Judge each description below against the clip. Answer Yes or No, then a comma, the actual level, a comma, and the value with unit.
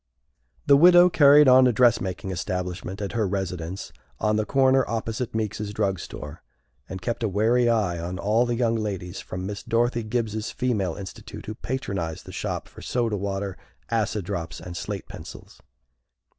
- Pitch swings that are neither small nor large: Yes, average, 4.0 semitones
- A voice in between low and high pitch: No, low, 105 Hz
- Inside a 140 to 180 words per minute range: Yes, average, 170 wpm